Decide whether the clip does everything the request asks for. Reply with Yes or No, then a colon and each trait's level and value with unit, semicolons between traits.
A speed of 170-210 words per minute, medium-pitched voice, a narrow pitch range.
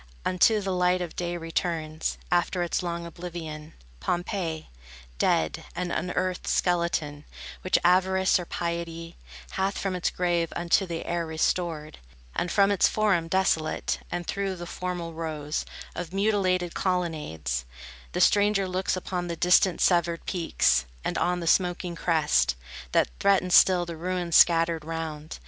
No: average, 140 wpm; medium, 175 Hz; narrow, 1.8 semitones